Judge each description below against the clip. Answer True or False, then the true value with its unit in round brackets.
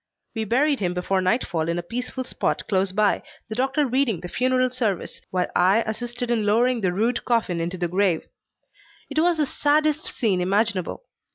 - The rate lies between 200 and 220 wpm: False (180 wpm)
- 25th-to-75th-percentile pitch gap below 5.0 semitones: False (5.5 semitones)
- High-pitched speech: True (220 Hz)